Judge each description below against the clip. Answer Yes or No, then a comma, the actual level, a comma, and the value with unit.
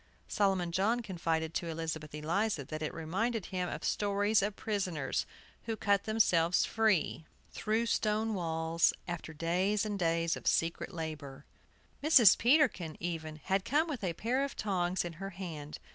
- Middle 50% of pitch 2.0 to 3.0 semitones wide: No, average, 4.6 semitones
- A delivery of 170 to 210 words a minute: No, average, 155 wpm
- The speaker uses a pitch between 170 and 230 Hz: Yes, medium, 185 Hz